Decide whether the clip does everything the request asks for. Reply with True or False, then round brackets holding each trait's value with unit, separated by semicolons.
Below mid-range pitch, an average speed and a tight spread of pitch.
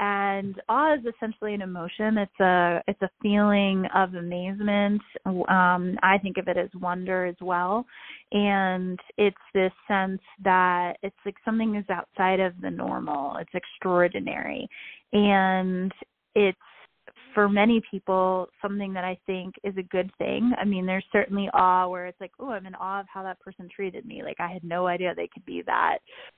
False (190 Hz; 175 wpm; 1.8 semitones)